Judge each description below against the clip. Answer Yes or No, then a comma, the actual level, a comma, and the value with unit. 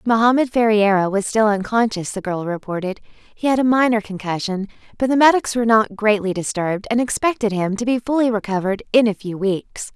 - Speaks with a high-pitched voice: Yes, high, 215 Hz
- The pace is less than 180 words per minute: No, average, 185 wpm